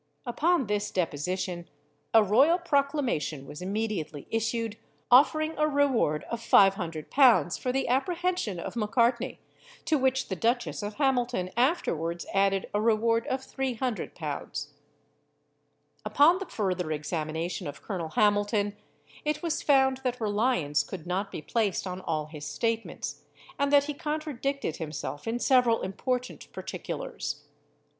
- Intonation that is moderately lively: No, wide, 6.5 semitones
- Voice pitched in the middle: No, high, 225 Hz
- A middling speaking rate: No, slow, 130 wpm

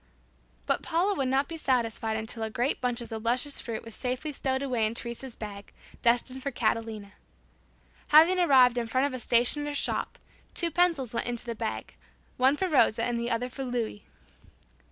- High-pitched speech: Yes, high, 245 Hz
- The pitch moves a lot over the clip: No, average, 3.3 semitones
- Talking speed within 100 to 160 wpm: No, average, 185 wpm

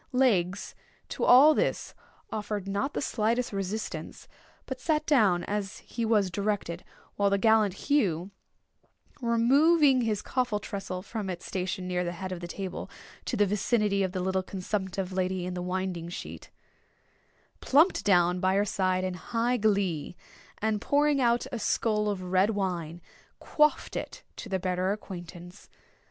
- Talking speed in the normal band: Yes, average, 155 wpm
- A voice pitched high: Yes, high, 200 Hz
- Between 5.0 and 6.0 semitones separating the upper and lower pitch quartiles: No, average, 3.8 semitones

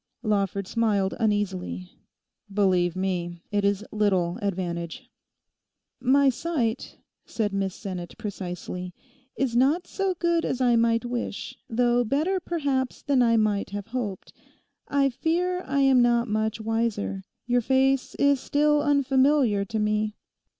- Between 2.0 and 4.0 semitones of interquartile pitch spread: No, average, 5.2 semitones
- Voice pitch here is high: Yes, high, 230 Hz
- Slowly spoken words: Yes, slow, 130 wpm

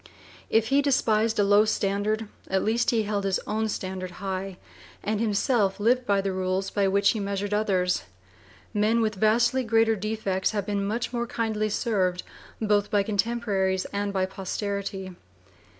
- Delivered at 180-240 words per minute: No, average, 160 wpm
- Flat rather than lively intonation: Yes, narrow, 2.3 semitones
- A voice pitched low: No, high, 205 Hz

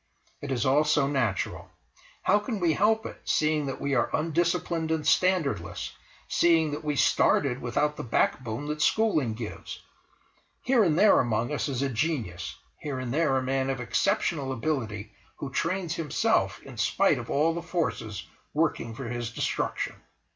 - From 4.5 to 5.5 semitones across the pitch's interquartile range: Yes, average, 5.0 semitones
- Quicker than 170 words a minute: No, average, 165 wpm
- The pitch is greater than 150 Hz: No, medium, 145 Hz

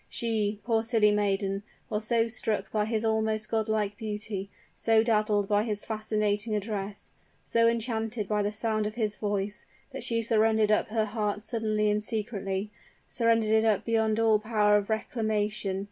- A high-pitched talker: Yes, high, 215 Hz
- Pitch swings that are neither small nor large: No, narrow, 1.3 semitones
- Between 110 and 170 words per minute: Yes, average, 160 wpm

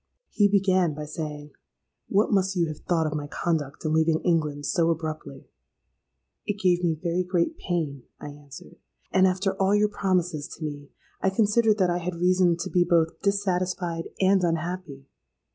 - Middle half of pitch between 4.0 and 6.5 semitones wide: No, average, 3.4 semitones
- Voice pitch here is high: No, medium, 175 Hz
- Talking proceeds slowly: No, average, 165 wpm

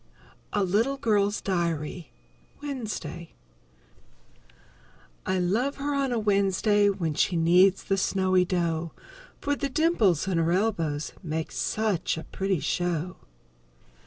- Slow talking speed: Yes, slow, 120 wpm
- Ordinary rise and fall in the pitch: Yes, average, 4.0 semitones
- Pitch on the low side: No, high, 190 Hz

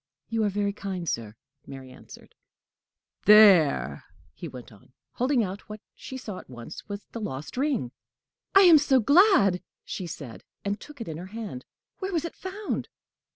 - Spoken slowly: No, average, 170 wpm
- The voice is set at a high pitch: Yes, high, 200 Hz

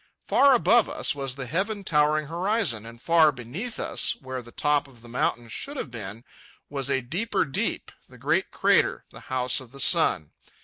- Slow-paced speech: No, average, 185 wpm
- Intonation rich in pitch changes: Yes, wide, 5.9 semitones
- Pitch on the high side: No, medium, 140 Hz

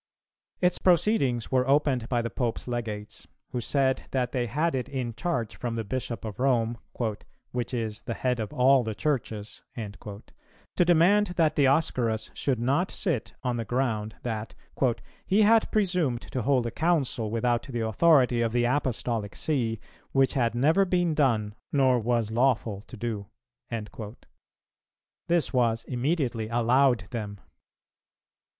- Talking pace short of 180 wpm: Yes, average, 145 wpm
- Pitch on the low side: Yes, low, 125 Hz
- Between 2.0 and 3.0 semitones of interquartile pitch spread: No, average, 3.5 semitones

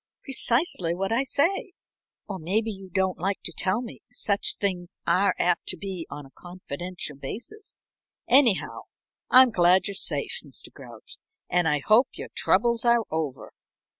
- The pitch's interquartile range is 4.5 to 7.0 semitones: Yes, average, 5.1 semitones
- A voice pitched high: Yes, high, 195 Hz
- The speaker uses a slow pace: No, average, 155 wpm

